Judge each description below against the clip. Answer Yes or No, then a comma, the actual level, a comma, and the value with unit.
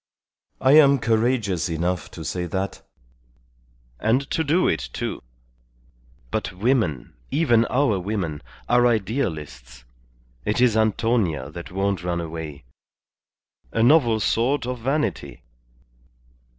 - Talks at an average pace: No, slow, 110 wpm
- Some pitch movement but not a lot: No, wide, 6.2 semitones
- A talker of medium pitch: No, low, 110 Hz